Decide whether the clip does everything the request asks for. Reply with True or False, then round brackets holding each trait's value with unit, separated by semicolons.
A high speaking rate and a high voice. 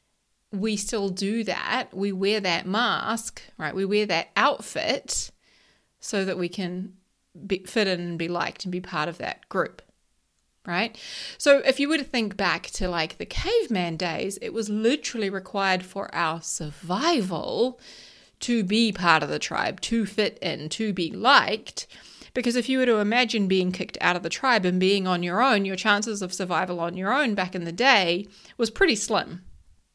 False (185 wpm; 195 Hz)